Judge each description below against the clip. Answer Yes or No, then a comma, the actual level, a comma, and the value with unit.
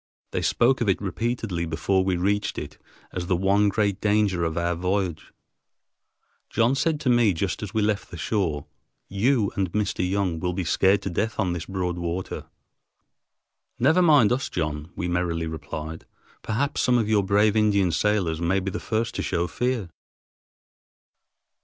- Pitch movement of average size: Yes, average, 3.8 semitones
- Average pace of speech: Yes, average, 170 wpm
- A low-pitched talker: Yes, very low, 95 Hz